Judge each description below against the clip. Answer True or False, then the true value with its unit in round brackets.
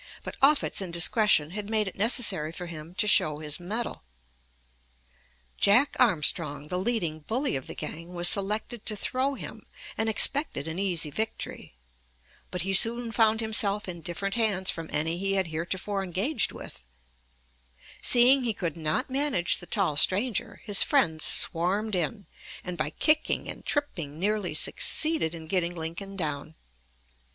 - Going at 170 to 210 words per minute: False (150 wpm)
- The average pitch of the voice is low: False (195 Hz)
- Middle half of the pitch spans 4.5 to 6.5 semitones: True (5.2 semitones)